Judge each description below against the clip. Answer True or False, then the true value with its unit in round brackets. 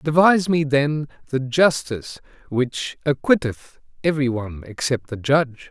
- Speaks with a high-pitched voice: False (140 Hz)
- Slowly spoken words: True (125 wpm)